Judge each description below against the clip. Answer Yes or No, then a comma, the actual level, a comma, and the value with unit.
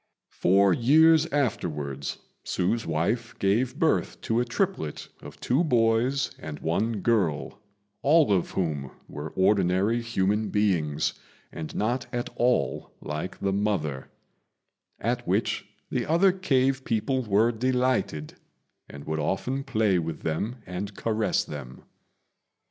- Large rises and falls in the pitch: Yes, wide, 6.7 semitones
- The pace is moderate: No, slow, 125 wpm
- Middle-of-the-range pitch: No, low, 105 Hz